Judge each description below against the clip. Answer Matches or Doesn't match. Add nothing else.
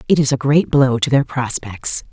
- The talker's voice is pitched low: Matches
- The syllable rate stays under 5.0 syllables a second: Matches